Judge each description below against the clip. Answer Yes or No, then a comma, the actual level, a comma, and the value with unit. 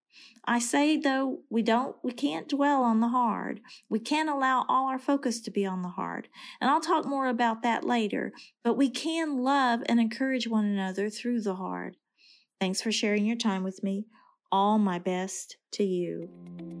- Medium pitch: No, high, 235 Hz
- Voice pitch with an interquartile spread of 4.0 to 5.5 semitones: Yes, average, 5.1 semitones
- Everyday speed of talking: Yes, average, 185 wpm